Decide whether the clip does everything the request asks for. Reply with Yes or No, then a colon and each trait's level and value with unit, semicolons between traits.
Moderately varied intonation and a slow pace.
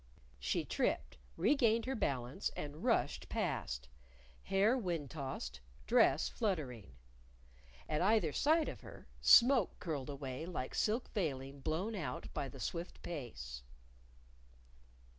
No: wide, 8.1 semitones; slow, 120 wpm